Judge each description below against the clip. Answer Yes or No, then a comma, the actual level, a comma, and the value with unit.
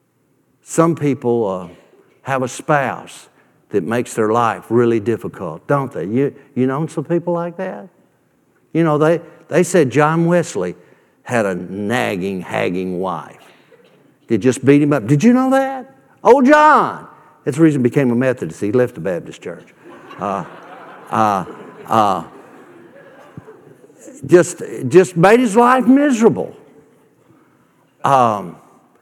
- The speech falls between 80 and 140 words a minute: Yes, slow, 135 wpm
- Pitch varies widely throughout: Yes, wide, 6.8 semitones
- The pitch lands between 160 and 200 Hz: No, medium, 145 Hz